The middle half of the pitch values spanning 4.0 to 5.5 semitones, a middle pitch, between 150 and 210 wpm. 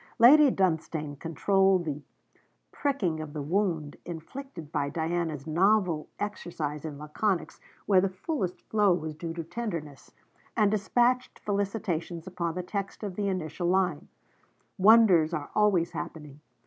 No: average, 4.4 semitones; medium, 175 Hz; slow, 135 wpm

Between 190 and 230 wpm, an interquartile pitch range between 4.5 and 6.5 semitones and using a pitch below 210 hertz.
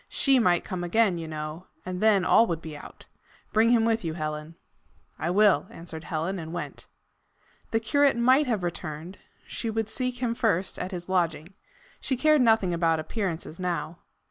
No: average, 175 wpm; wide, 5.4 semitones; medium, 185 Hz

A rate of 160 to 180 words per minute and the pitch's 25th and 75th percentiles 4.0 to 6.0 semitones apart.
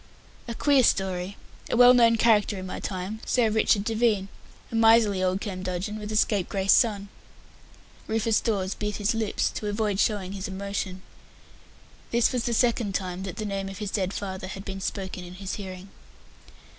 No: average, 175 wpm; average, 2.7 semitones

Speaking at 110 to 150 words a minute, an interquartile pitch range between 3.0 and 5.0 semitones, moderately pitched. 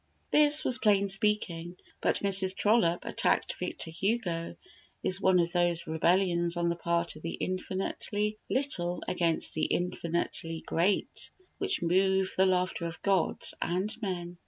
No: average, 140 wpm; narrow, 2.4 semitones; medium, 180 Hz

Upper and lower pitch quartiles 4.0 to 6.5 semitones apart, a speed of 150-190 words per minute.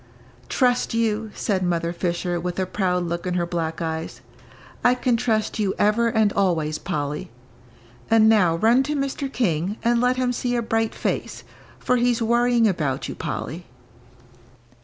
Yes: wide, 5.5 semitones; average, 160 wpm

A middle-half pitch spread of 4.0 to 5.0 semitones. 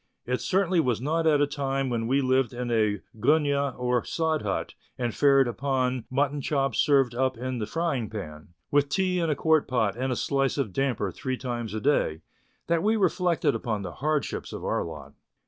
No: average, 3.5 semitones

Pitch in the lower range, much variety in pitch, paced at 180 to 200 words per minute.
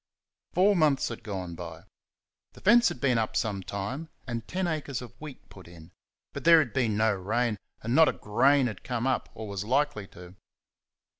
Yes: low, 115 Hz; wide, 6.2 semitones; average, 195 wpm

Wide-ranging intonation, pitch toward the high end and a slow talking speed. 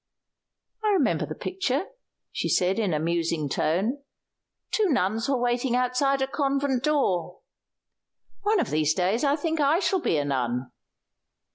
No: wide, 8.8 semitones; very high, 250 Hz; average, 150 wpm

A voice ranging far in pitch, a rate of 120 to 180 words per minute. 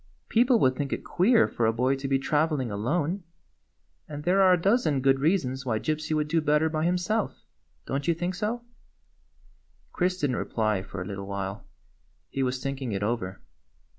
No: wide, 6.1 semitones; average, 195 wpm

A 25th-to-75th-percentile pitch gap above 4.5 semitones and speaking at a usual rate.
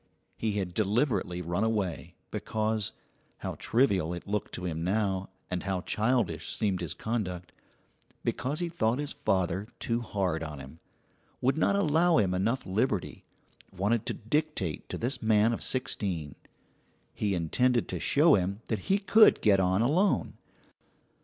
Yes: average, 5.3 semitones; average, 150 wpm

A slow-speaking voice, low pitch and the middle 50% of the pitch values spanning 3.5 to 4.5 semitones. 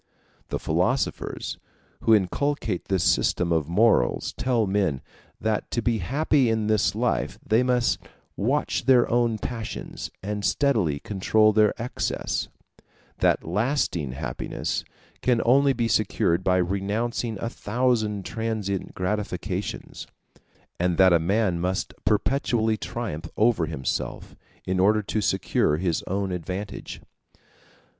Yes: slow, 120 wpm; low, 105 Hz; average, 4.1 semitones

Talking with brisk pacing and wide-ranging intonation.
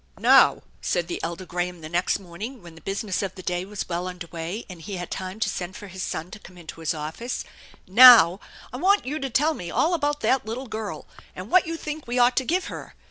Yes: fast, 245 wpm; wide, 6.3 semitones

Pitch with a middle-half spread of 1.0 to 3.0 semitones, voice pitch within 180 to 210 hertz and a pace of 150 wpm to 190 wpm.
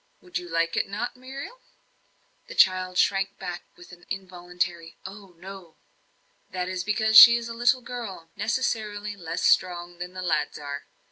No: average, 3.6 semitones; medium, 185 Hz; average, 160 wpm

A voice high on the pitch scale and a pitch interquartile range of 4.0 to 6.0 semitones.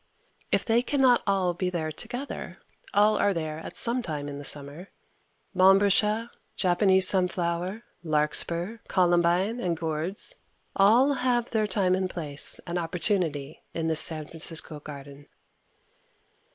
No: medium, 180 Hz; average, 4.6 semitones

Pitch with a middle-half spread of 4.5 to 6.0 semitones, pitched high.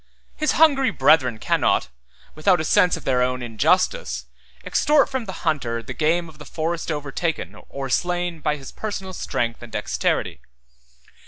No: wide, 5.4 semitones; medium, 160 Hz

